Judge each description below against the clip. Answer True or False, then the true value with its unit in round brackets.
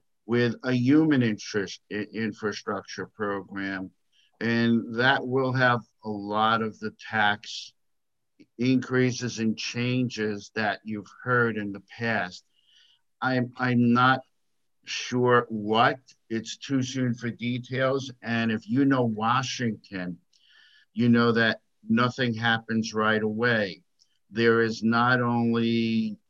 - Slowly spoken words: True (115 wpm)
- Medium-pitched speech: False (115 Hz)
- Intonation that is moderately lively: False (2.3 semitones)